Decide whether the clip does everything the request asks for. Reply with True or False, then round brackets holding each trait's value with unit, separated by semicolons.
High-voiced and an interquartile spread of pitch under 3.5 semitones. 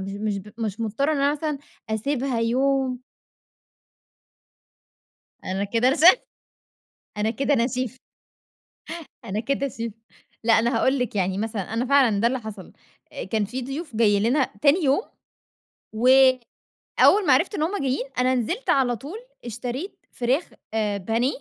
False (245 Hz; 3.9 semitones)